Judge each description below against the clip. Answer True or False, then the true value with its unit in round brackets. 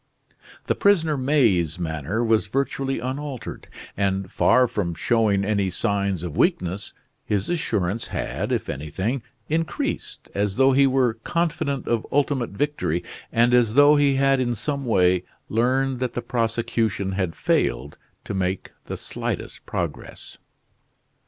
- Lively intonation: True (5.8 semitones)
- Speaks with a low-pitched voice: True (115 Hz)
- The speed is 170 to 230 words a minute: False (135 wpm)